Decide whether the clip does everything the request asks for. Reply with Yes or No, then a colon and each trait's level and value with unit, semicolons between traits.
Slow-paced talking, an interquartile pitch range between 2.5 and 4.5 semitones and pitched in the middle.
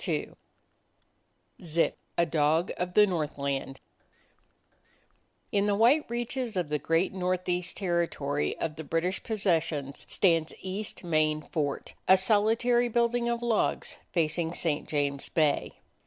No: slow, 125 wpm; average, 5.2 semitones; medium, 175 Hz